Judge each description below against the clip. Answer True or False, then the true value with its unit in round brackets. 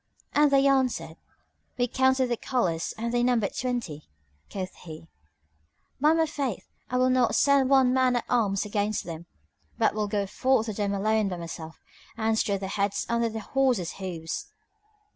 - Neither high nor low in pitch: False (225 Hz)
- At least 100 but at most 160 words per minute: False (170 wpm)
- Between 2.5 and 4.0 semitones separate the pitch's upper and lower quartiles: False (4.7 semitones)